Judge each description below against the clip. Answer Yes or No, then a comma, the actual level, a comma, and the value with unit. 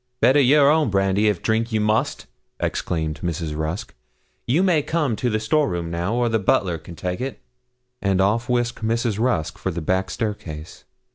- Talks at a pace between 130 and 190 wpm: Yes, average, 185 wpm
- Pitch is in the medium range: No, low, 105 Hz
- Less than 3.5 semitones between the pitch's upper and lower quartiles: No, wide, 5.4 semitones